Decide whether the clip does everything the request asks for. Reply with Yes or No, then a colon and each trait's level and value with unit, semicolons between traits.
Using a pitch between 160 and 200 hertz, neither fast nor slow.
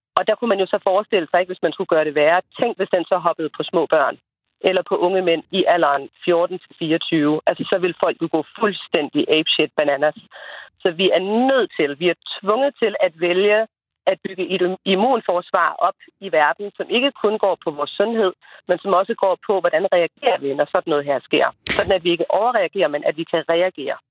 Yes: medium, 185 Hz; average, 215 wpm